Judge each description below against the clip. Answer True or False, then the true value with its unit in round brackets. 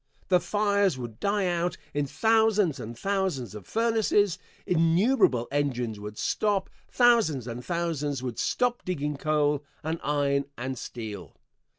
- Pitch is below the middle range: False (155 Hz)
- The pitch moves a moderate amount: False (7.7 semitones)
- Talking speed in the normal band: False (130 wpm)